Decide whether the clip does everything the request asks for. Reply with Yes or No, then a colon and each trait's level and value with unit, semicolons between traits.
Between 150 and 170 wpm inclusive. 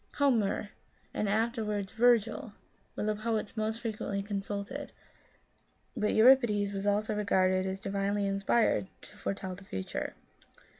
No: slow, 135 wpm